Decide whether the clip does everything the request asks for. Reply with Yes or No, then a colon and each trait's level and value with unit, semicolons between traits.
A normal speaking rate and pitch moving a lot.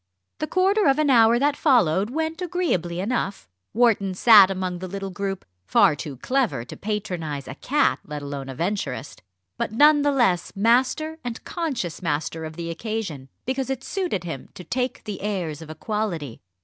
Yes: average, 175 wpm; wide, 7.8 semitones